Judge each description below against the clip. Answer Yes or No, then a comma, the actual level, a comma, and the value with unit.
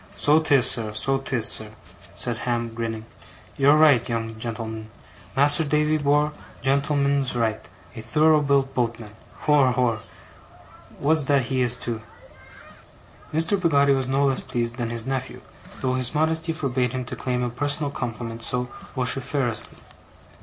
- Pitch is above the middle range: No, low, 130 Hz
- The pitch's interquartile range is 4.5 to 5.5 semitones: No, average, 3.5 semitones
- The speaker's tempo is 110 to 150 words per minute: Yes, average, 145 wpm